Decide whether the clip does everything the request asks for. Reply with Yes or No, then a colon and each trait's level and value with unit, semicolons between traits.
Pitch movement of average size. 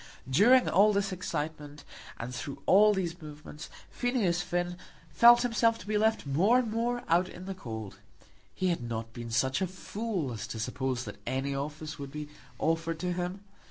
No: wide, 6.3 semitones